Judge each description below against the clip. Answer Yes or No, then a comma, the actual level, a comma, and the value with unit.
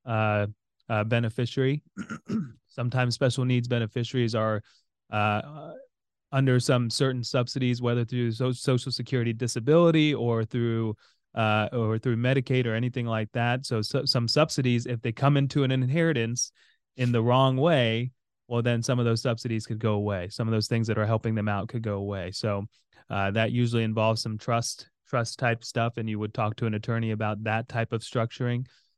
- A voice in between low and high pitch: No, low, 120 Hz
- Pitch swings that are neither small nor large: No, narrow, 2.3 semitones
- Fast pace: No, average, 180 wpm